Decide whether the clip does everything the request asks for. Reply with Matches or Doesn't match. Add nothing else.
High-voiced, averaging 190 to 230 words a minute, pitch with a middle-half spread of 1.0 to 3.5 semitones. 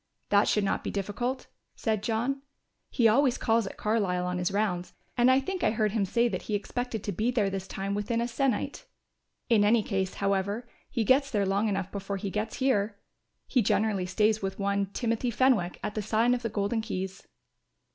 Matches